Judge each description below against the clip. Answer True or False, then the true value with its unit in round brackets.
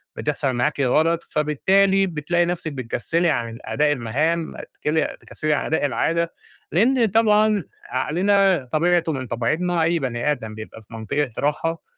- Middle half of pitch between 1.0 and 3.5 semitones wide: False (4.9 semitones)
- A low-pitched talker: False (155 Hz)